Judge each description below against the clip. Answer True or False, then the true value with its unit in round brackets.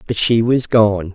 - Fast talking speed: True (210 wpm)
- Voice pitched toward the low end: True (110 Hz)